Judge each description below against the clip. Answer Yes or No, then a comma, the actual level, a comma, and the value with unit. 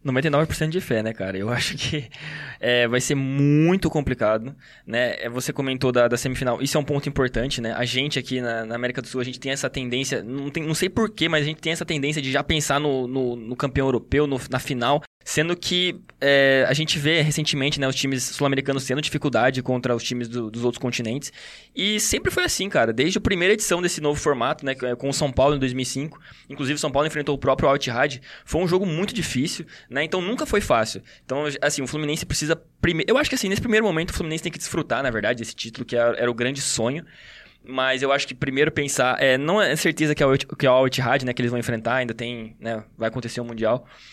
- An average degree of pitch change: Yes, average, 3.5 semitones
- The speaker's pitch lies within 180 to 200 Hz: No, medium, 140 Hz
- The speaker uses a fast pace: Yes, fast, 235 wpm